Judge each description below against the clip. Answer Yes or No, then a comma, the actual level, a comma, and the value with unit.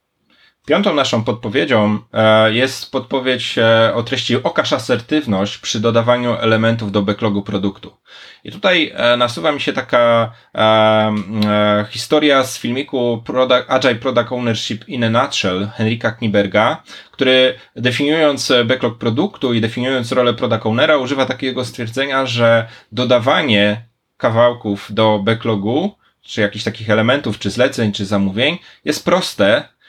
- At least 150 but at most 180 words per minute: No, average, 120 wpm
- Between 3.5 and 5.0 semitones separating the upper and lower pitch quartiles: No, average, 2.9 semitones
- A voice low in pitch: Yes, low, 115 Hz